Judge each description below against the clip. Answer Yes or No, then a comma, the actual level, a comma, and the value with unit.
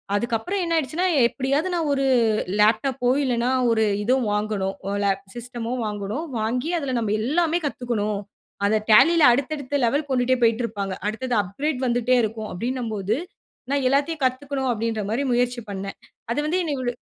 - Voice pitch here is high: Yes, high, 245 Hz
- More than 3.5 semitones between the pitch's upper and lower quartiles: Yes, average, 4.2 semitones